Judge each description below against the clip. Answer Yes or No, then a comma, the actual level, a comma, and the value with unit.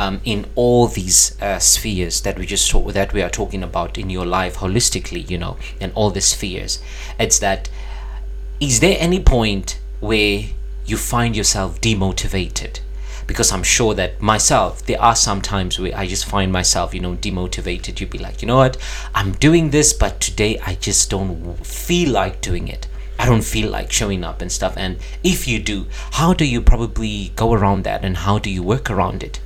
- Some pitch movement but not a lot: Yes, average, 3.6 semitones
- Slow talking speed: No, average, 200 wpm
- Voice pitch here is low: Yes, low, 100 Hz